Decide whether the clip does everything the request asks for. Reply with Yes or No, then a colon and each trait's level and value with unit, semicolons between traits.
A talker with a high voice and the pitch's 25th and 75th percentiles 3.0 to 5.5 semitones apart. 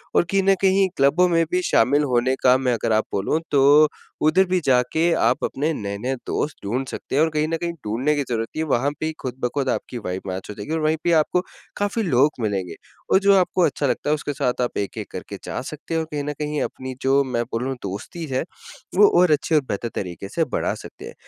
No: medium, 140 Hz; average, 4.9 semitones